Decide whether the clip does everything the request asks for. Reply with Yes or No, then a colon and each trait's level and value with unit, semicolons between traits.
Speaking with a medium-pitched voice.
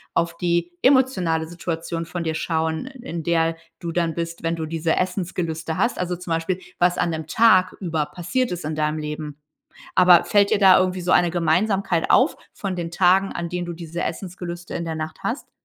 Yes: medium, 170 Hz